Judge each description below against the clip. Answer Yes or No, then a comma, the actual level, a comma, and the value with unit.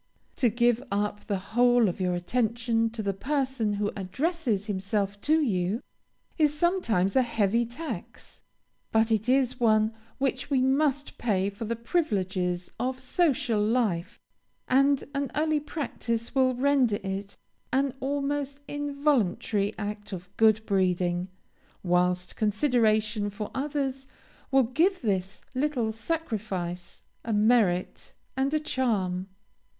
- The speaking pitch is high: Yes, high, 230 Hz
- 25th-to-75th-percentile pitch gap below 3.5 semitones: No, average, 5.1 semitones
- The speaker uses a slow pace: Yes, slow, 125 wpm